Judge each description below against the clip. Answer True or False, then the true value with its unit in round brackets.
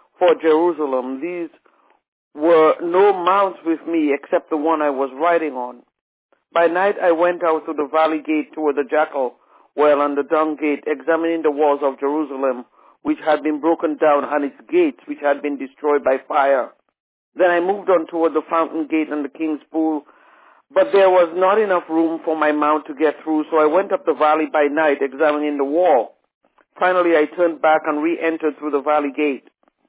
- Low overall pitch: False (155 Hz)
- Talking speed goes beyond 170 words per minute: True (195 wpm)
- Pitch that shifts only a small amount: True (2.0 semitones)